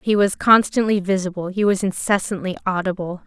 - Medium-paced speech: Yes, average, 145 wpm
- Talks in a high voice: Yes, high, 195 Hz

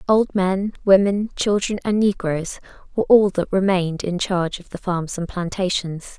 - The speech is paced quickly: No, average, 165 wpm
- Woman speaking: Yes, female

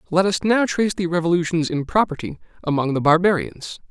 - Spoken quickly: No, average, 170 wpm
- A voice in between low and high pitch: Yes, medium, 175 Hz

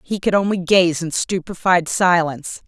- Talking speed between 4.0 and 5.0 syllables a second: Yes, 4.7 syllables/s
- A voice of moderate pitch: Yes, medium, 180 Hz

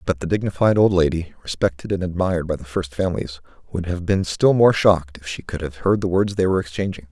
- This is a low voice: Yes, very low, 90 Hz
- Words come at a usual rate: No, fast, 235 wpm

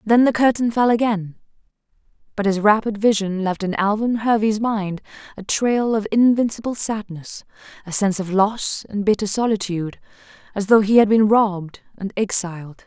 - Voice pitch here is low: No, high, 210 Hz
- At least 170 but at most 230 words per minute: No, average, 160 wpm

